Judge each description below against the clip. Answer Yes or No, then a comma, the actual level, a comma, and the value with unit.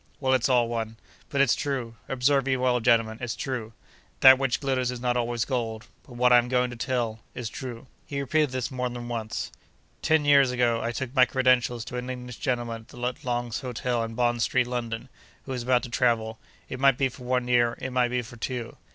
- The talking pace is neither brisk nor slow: No, fast, 215 wpm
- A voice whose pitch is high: No, low, 125 Hz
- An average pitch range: No, narrow, 1.5 semitones